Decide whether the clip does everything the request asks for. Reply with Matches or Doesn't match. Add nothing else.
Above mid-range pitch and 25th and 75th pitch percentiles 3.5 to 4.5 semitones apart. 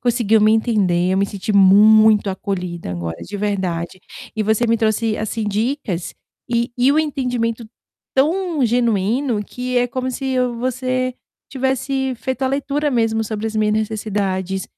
Matches